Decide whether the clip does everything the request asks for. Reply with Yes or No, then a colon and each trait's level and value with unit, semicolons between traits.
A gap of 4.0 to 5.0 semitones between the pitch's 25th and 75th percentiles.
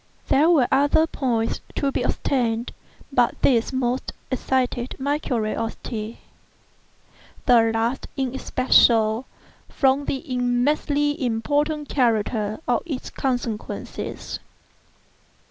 No: average, 3.2 semitones